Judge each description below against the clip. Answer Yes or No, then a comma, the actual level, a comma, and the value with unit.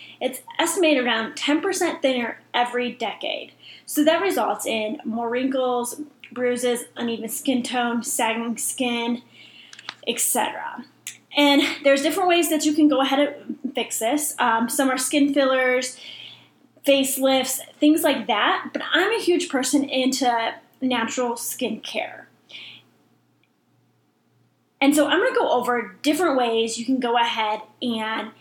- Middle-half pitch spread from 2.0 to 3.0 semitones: No, average, 3.8 semitones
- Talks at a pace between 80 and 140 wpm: Yes, slow, 135 wpm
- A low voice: No, very high, 260 Hz